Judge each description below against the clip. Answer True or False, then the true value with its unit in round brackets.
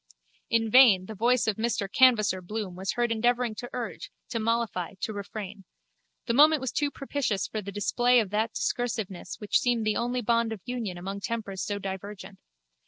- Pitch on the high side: True (220 Hz)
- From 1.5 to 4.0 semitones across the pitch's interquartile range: True (3.3 semitones)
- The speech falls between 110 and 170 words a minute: False (180 wpm)